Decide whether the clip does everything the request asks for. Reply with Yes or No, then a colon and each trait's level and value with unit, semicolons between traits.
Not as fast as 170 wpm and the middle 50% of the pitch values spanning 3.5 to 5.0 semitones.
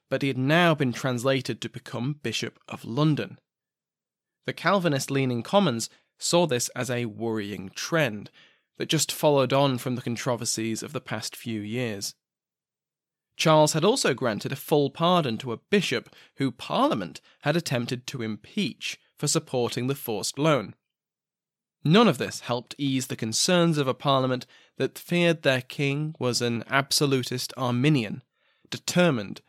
Yes: average, 150 wpm; average, 3.9 semitones